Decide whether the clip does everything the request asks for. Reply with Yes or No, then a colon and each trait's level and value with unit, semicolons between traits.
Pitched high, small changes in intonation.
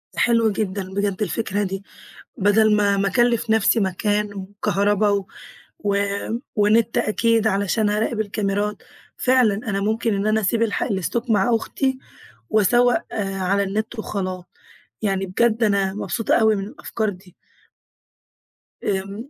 Yes: high, 205 Hz; narrow, 2.1 semitones